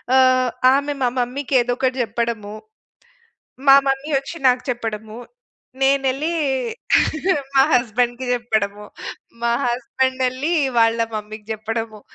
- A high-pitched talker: Yes, high, 245 Hz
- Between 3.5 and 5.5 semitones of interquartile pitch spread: No, average, 2.8 semitones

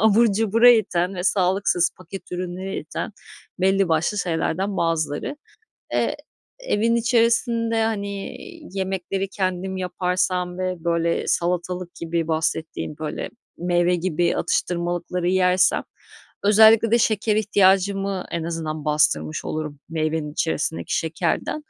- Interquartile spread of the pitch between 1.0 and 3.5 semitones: Yes, average, 3.1 semitones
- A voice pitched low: No, medium, 180 Hz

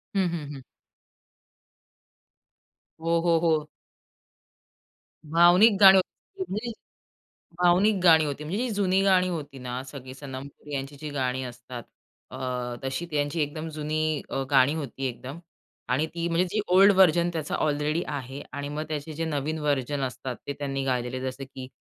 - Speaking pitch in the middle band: Yes, medium, 150 Hz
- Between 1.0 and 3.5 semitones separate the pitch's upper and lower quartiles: No, average, 3.9 semitones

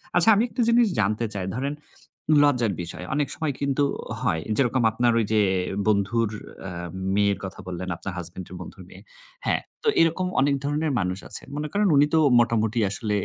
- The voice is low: Yes, low, 120 Hz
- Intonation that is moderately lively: No, wide, 6.6 semitones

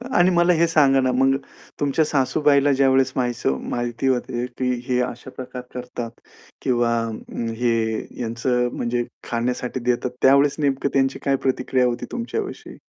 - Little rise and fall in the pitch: Yes, narrow, 2.2 semitones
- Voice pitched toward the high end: No, low, 130 Hz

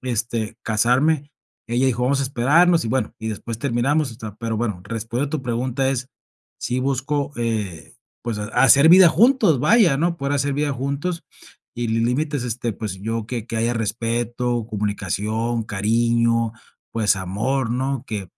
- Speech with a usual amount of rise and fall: Yes, average, 3.5 semitones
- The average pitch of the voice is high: No, low, 120 Hz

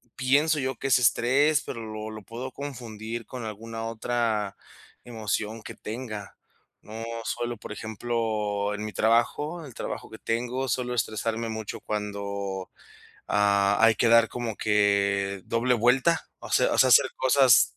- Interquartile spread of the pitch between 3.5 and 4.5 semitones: No, narrow, 2.6 semitones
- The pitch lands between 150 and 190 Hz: No, low, 115 Hz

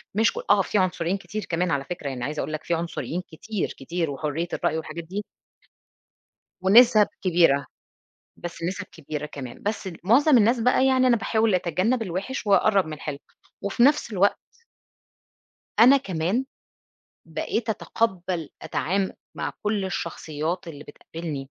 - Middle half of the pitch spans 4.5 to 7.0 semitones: Yes, average, 5.2 semitones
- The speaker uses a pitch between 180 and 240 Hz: Yes, medium, 185 Hz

